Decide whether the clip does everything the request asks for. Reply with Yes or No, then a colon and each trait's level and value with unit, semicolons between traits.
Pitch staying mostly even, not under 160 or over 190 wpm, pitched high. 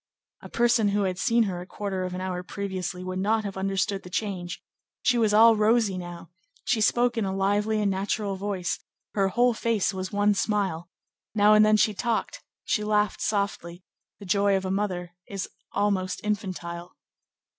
Yes: narrow, 2.3 semitones; average, 180 wpm; high, 200 Hz